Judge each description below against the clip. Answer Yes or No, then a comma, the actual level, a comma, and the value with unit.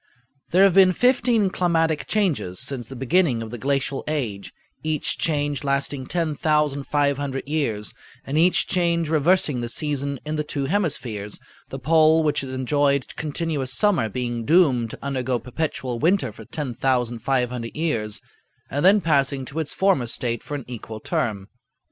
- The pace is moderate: Yes, average, 150 wpm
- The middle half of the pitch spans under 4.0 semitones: No, average, 4.3 semitones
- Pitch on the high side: No, medium, 140 Hz